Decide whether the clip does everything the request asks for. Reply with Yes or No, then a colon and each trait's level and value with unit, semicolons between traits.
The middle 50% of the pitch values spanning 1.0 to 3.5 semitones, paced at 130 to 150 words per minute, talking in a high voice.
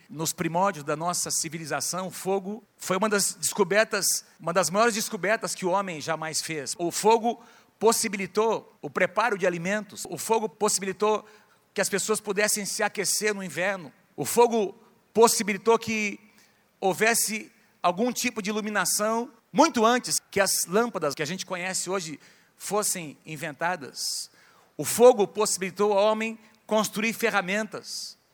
Yes: average, 3.2 semitones; average, 140 wpm; high, 205 Hz